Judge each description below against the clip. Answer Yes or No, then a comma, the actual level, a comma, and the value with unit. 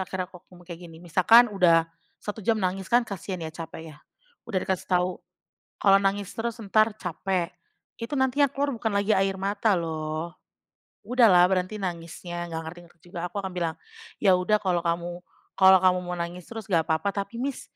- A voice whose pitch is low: No, medium, 185 Hz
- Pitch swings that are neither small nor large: Yes, average, 3.2 semitones